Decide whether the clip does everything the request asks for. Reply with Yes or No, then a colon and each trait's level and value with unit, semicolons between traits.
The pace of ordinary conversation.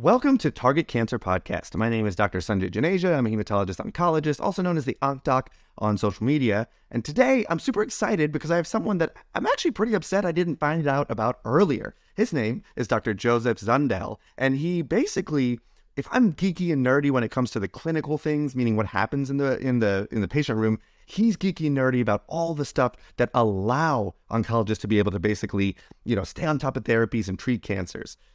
No: fast, 215 wpm